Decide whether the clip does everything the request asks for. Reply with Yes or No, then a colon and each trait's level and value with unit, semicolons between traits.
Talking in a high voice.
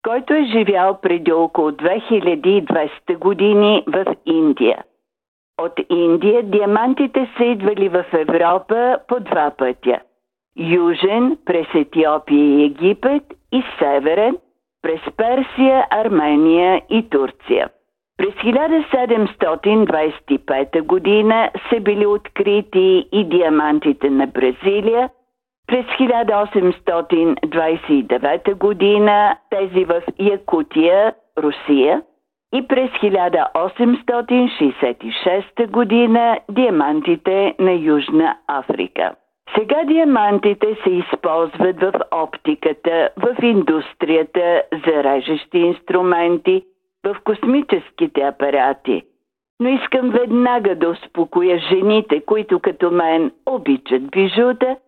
Yes: high, 200 Hz